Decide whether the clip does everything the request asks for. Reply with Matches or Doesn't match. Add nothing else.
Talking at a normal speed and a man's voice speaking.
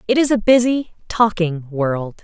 Doesn't match